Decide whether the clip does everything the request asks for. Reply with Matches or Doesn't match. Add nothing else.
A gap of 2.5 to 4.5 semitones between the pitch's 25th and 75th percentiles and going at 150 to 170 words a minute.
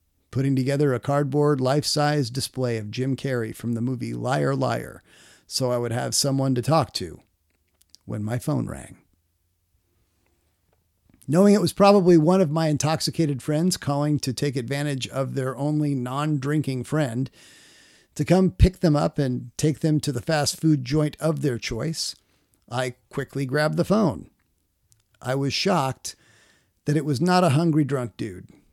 Doesn't match